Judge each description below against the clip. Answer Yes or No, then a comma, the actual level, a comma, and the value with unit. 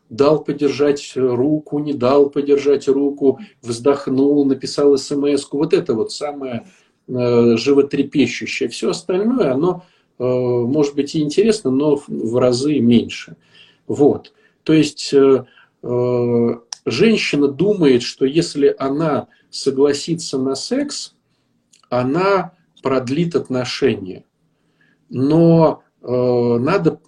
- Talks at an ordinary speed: No, slow, 95 wpm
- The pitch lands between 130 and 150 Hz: Yes, medium, 140 Hz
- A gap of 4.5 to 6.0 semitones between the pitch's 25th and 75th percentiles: No, average, 3.1 semitones